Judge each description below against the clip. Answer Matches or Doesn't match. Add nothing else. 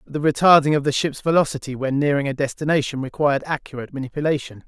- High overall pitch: Doesn't match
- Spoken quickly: Doesn't match